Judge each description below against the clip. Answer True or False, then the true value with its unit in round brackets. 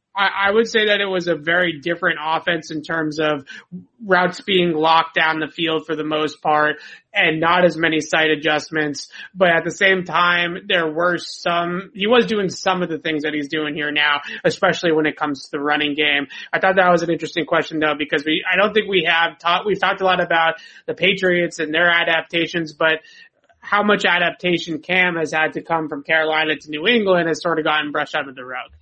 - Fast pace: True (220 wpm)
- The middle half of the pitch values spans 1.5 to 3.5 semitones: True (2.6 semitones)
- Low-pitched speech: False (165 Hz)